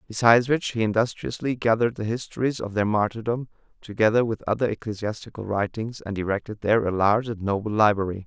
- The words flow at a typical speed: Yes, average, 165 wpm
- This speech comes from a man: Yes, male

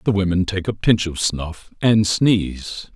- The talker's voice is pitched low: Yes, very low, 95 Hz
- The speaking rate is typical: Yes, average, 180 wpm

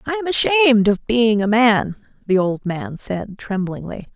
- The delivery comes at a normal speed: Yes, average, 175 wpm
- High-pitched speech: Yes, high, 220 Hz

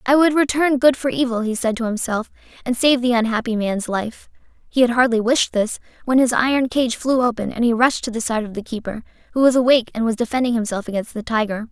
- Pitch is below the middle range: No, high, 240 Hz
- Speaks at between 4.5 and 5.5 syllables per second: No, 6.0 syllables/s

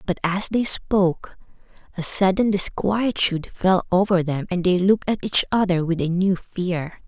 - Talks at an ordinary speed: Yes, average, 170 wpm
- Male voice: No, female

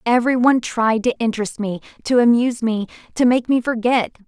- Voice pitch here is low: No, high, 235 Hz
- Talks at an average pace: Yes, average, 180 wpm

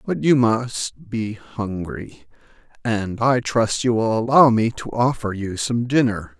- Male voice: Yes, male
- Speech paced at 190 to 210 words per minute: No, average, 160 wpm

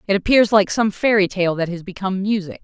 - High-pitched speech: Yes, high, 195 Hz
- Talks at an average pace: No, fast, 230 wpm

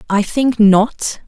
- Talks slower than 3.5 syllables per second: Yes, 2.8 syllables/s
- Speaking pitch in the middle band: No, high, 220 Hz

